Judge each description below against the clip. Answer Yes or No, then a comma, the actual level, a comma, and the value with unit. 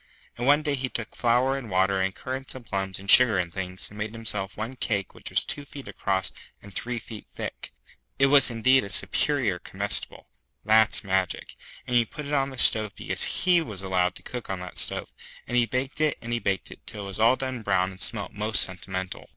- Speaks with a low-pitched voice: Yes, low, 110 Hz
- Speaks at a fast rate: Yes, fast, 220 wpm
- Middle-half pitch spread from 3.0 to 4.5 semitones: No, average, 5.1 semitones